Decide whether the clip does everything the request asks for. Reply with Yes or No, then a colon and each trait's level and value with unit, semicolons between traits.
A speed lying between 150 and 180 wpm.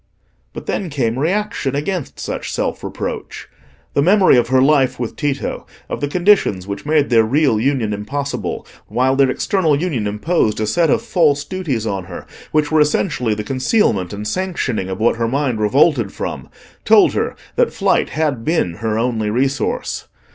Yes: average, 170 wpm